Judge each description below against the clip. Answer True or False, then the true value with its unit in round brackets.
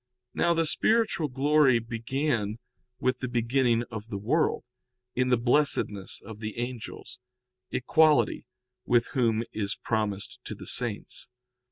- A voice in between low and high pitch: False (120 Hz)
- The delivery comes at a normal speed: False (130 wpm)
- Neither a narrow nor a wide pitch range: True (4.3 semitones)